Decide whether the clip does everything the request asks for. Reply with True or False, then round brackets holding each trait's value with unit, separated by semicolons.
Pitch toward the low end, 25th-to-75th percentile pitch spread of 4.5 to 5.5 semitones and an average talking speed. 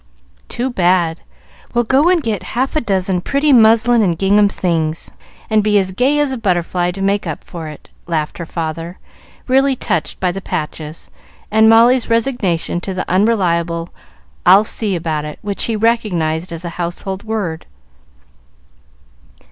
False (190 Hz; 5.1 semitones; 155 wpm)